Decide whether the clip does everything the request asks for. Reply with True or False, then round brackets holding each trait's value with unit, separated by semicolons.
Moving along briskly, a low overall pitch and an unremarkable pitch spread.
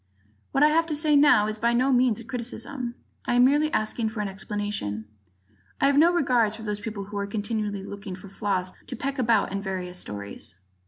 False (210 wpm; 220 Hz; 4.2 semitones)